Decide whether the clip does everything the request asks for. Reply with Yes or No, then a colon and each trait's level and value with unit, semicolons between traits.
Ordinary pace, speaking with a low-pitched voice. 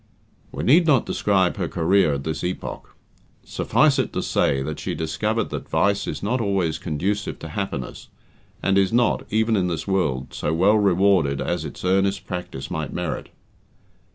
Yes: average, 170 wpm; very low, 95 Hz